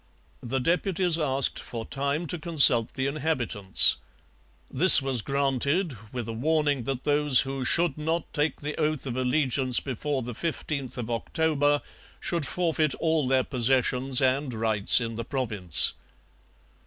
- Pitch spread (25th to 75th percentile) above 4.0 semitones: No, average, 3.5 semitones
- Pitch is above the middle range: No, low, 135 Hz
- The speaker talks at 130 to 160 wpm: Yes, average, 140 wpm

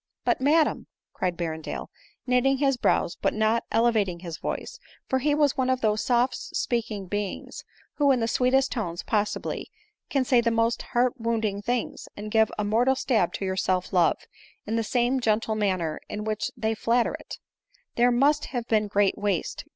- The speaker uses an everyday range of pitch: Yes, average, 3.5 semitones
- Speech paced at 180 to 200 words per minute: Yes, average, 195 wpm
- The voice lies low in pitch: No, high, 225 Hz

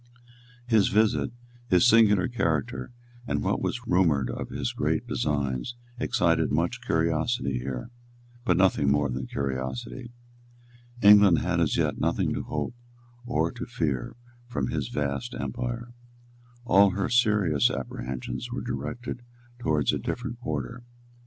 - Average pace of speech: No, slow, 130 wpm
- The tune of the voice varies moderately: No, wide, 9.0 semitones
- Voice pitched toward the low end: Yes, very low, 90 Hz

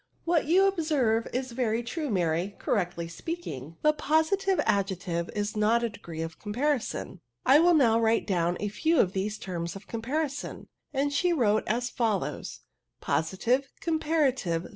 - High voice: Yes, high, 230 Hz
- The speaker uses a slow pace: No, average, 175 wpm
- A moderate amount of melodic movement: No, wide, 7.8 semitones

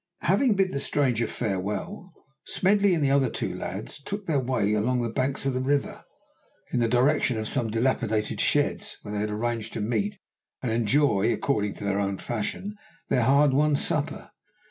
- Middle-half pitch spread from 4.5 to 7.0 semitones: Yes, average, 4.9 semitones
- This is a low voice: Yes, low, 125 Hz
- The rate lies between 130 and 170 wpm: No, average, 180 wpm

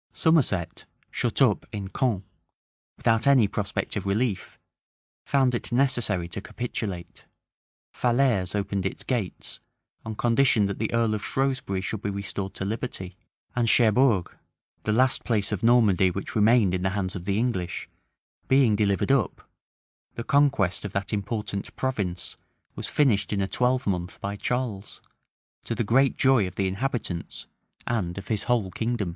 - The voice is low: Yes, low, 105 Hz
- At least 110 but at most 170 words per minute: Yes, average, 150 wpm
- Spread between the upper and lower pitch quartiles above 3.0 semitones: Yes, average, 4.0 semitones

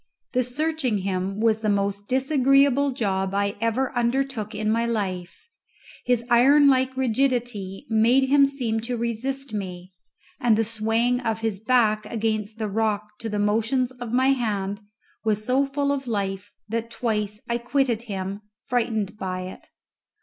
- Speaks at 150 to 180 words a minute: Yes, average, 155 wpm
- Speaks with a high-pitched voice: Yes, high, 225 Hz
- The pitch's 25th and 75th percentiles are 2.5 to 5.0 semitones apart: Yes, average, 3.5 semitones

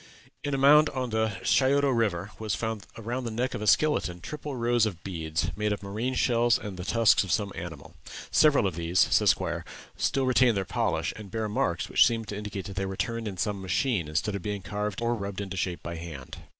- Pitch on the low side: Yes, low, 105 Hz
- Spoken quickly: Yes, fast, 225 wpm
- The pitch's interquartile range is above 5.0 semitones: No, average, 4.1 semitones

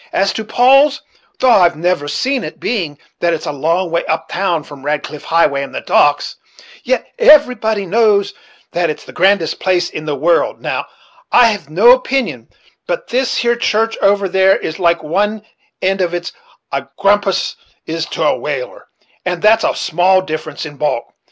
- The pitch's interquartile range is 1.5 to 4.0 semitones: No, wide, 5.4 semitones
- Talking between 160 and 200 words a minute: Yes, average, 185 wpm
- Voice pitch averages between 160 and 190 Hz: Yes, medium, 185 Hz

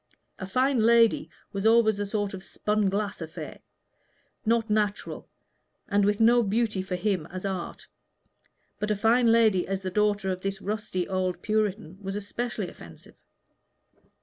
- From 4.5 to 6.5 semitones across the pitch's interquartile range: No, narrow, 2.4 semitones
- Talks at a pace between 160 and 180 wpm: No, average, 150 wpm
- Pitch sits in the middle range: No, high, 205 Hz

